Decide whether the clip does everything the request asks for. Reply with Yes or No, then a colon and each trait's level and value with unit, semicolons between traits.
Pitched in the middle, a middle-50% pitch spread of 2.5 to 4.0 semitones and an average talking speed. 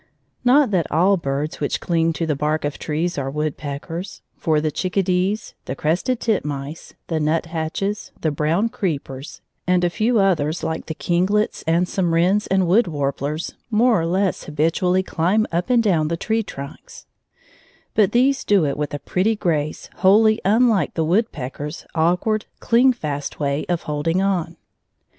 No: medium, 170 Hz; average, 4.8 semitones; average, 160 wpm